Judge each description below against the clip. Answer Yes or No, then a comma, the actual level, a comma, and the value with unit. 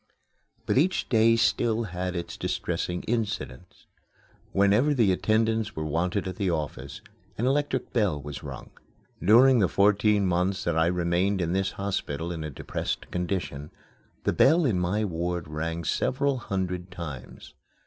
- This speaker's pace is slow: No, average, 150 wpm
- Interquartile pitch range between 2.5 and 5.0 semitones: Yes, average, 4.4 semitones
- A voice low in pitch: Yes, very low, 95 Hz